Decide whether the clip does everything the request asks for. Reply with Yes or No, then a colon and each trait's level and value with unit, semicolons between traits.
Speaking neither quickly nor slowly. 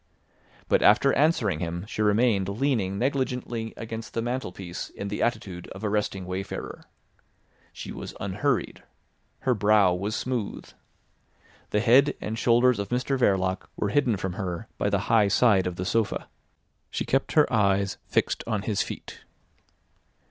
Yes: average, 150 wpm